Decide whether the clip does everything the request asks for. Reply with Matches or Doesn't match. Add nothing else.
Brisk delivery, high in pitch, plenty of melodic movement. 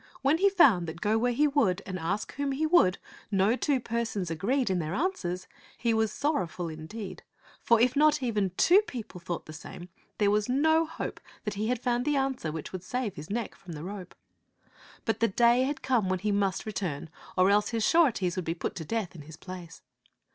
Matches